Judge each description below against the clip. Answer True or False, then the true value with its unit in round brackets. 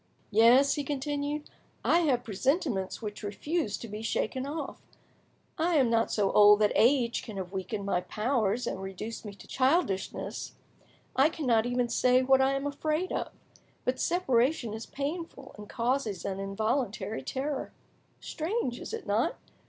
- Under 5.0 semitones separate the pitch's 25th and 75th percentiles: False (5.3 semitones)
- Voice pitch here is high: True (245 Hz)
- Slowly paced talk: False (155 wpm)